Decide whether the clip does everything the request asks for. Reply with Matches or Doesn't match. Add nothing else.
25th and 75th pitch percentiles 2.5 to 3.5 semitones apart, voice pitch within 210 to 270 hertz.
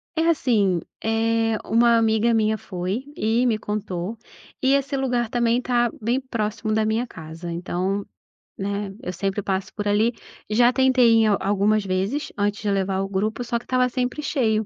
Matches